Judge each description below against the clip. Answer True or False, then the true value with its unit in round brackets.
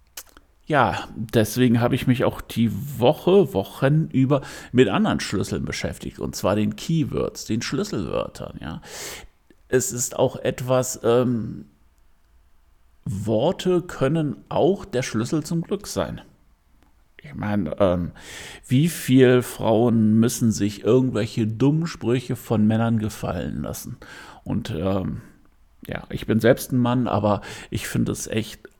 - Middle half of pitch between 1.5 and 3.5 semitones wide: False (3.9 semitones)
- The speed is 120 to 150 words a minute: True (130 wpm)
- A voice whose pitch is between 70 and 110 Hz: False (120 Hz)